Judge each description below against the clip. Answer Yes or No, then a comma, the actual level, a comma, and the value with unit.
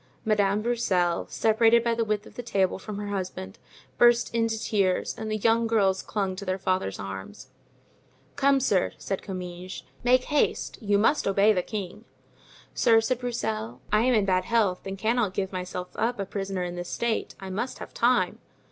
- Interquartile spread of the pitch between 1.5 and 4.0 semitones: Yes, average, 3.7 semitones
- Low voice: No, high, 205 Hz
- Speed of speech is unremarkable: Yes, average, 185 wpm